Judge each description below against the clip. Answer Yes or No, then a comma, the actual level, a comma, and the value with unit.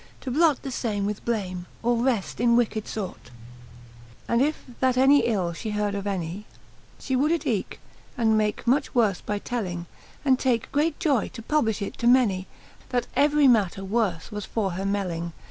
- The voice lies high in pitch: Yes, high, 220 Hz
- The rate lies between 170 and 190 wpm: Yes, average, 185 wpm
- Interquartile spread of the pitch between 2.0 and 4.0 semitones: No, average, 4.4 semitones